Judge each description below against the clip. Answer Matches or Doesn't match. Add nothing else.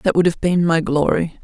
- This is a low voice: Doesn't match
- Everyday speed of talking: Doesn't match